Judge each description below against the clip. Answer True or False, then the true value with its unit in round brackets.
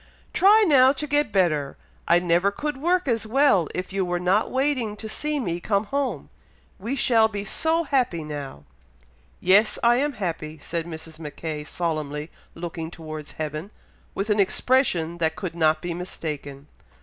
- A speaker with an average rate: True (160 wpm)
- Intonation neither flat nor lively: False (8.0 semitones)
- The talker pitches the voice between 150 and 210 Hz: True (185 Hz)